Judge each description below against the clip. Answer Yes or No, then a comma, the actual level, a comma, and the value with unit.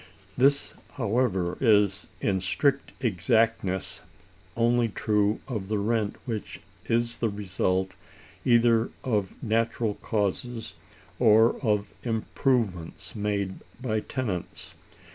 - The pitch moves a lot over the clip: No, average, 2.7 semitones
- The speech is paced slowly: Yes, slow, 100 wpm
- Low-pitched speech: Yes, low, 110 Hz